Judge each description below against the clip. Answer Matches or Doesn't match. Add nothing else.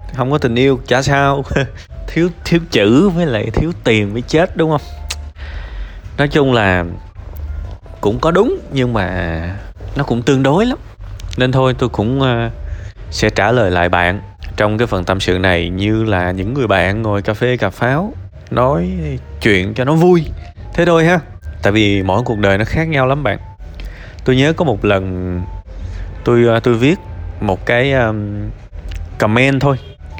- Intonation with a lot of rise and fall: Matches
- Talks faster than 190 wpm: Doesn't match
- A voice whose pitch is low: Matches